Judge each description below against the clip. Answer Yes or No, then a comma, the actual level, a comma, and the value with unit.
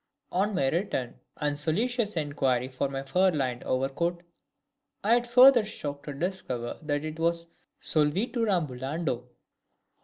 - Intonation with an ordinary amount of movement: No, wide, 6.0 semitones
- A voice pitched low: No, medium, 155 Hz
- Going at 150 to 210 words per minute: No, slow, 135 wpm